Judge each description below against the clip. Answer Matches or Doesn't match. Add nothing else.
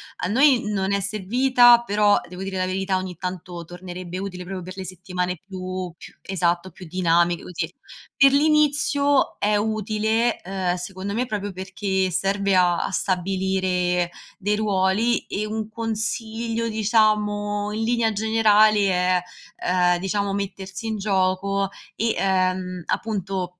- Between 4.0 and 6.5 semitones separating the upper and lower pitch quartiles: Doesn't match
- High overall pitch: Matches